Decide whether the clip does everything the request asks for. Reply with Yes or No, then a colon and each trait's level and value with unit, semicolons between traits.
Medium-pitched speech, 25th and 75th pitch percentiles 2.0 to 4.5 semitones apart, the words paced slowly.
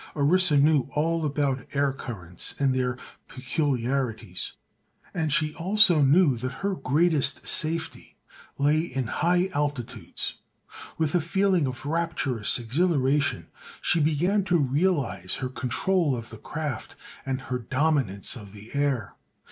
Yes: medium, 145 Hz; average, 4.2 semitones; slow, 130 wpm